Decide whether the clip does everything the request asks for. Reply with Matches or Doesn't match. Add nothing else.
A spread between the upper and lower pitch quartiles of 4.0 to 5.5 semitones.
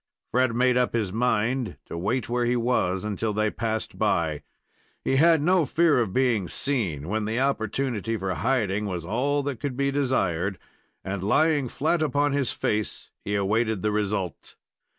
Matches